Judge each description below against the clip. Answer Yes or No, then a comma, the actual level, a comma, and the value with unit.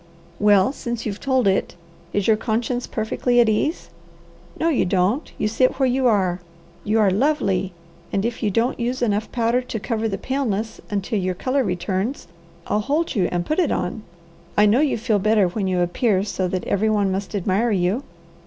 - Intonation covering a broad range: No, average, 4.0 semitones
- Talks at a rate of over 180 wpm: Yes, average, 190 wpm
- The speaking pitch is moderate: No, high, 215 Hz